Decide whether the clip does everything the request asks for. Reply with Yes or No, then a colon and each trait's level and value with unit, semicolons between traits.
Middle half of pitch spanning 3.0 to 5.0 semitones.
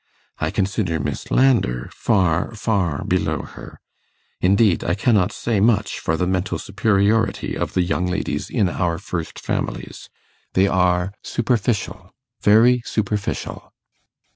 Yes: average, 3.4 semitones